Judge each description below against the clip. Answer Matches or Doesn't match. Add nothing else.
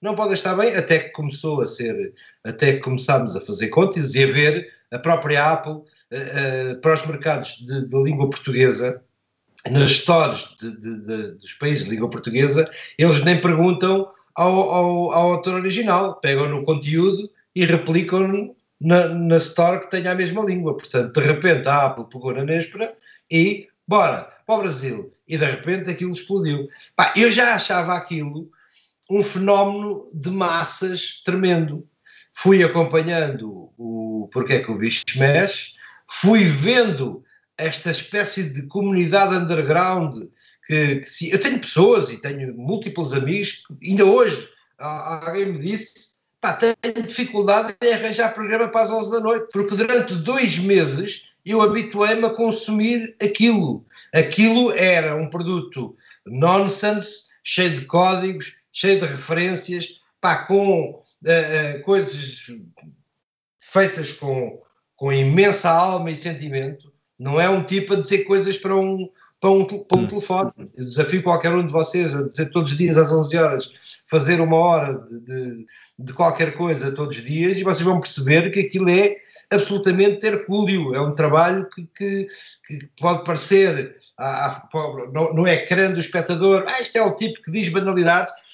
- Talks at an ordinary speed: Matches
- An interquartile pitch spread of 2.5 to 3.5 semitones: Doesn't match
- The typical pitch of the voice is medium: Matches